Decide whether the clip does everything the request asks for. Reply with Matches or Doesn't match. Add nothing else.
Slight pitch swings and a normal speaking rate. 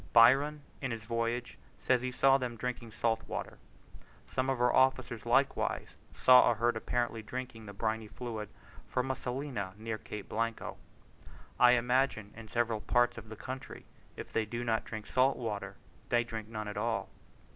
Matches